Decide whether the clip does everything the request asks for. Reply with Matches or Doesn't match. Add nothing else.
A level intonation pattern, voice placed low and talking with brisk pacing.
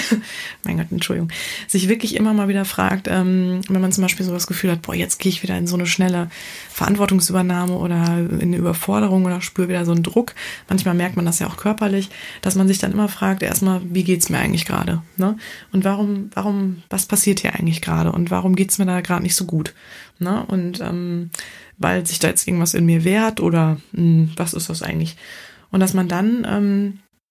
Doesn't match